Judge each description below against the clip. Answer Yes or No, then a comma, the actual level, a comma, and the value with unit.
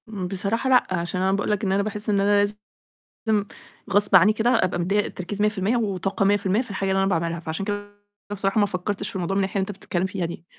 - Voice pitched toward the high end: Yes, high, 200 Hz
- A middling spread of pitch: No, narrow, 1.7 semitones